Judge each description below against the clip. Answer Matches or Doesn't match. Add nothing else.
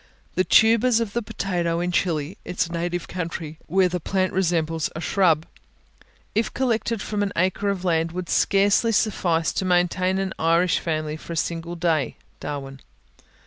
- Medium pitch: Matches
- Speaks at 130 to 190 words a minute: Matches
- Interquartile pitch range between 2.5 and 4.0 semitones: Matches